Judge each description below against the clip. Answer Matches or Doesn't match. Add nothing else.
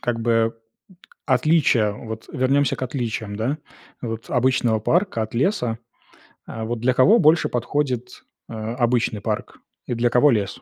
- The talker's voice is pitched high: Doesn't match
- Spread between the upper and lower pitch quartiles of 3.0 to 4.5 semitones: Doesn't match